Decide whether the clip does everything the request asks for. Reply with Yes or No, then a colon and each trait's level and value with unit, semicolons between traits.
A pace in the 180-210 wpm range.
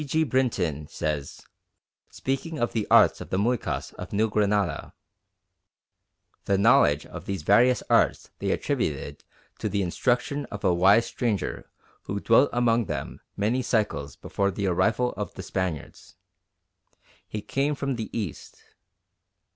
No: average, 140 wpm